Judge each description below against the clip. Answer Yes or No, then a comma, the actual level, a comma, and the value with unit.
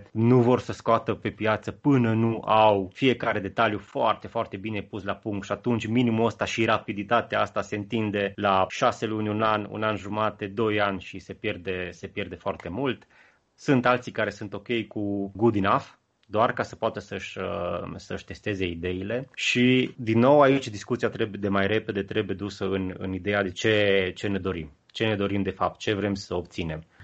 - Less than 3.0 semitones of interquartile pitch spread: Yes, narrow, 2.6 semitones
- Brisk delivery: Yes, fast, 195 wpm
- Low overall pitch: Yes, low, 105 Hz